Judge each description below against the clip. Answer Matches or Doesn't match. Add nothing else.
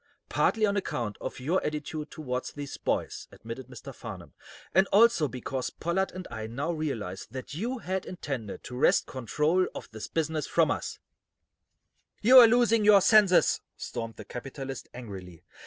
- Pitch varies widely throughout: Matches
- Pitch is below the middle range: Doesn't match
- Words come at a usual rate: Matches